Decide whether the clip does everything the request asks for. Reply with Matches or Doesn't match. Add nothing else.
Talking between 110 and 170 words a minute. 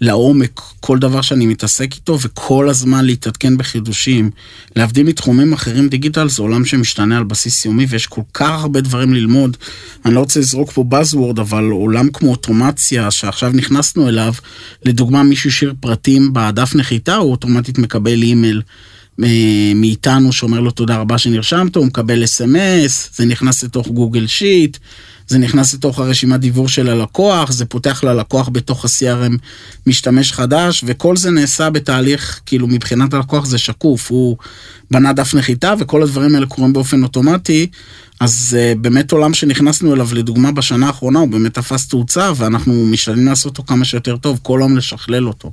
Matches